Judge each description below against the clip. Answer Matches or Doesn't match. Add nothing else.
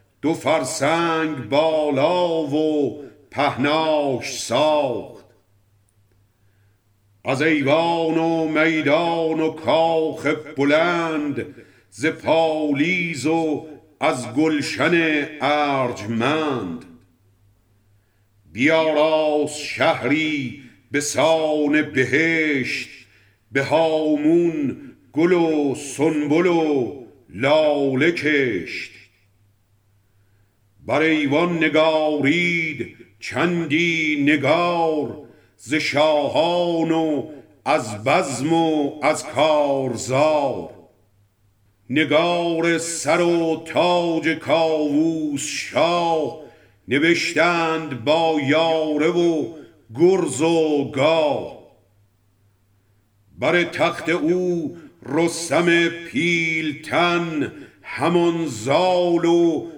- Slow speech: Matches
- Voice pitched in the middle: Matches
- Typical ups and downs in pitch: Matches